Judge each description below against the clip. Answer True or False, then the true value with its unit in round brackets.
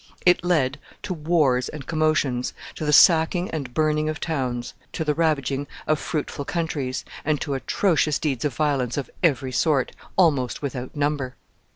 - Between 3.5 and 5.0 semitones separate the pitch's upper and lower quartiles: False (3.1 semitones)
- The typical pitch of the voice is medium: True (150 Hz)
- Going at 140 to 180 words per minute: True (160 wpm)